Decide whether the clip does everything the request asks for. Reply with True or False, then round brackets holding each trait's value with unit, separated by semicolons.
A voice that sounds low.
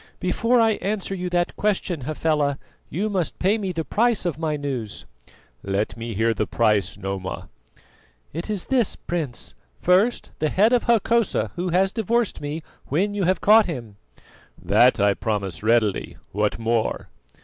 False (165 Hz)